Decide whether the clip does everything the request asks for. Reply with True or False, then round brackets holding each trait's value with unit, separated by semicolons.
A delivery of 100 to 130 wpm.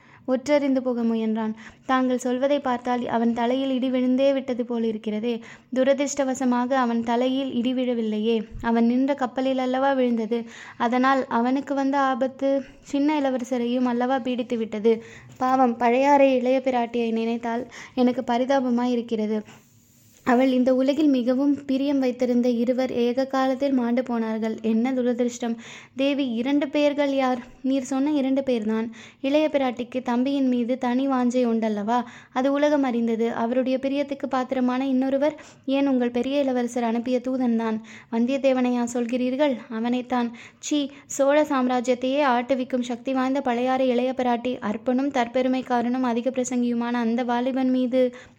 True (125 wpm)